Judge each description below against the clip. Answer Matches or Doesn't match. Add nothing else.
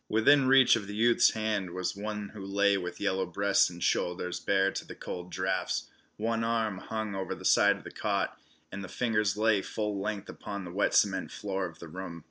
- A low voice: Matches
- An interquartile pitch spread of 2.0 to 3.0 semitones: Matches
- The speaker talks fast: Matches